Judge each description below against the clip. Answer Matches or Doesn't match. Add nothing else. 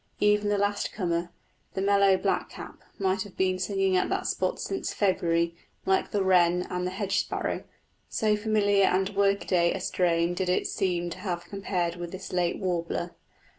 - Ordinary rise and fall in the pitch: Doesn't match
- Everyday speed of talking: Matches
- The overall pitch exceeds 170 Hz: Matches